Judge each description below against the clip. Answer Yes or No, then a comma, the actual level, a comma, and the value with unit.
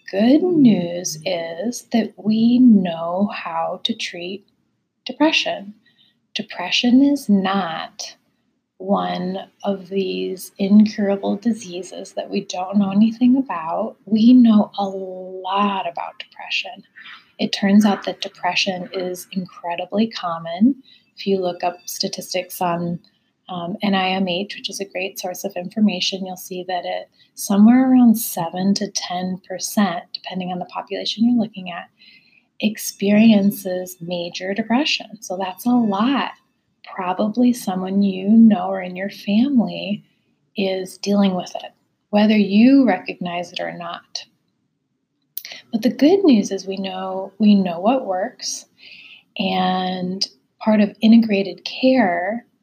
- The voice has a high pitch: Yes, high, 200 Hz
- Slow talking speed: Yes, slow, 125 wpm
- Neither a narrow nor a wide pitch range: Yes, average, 3.6 semitones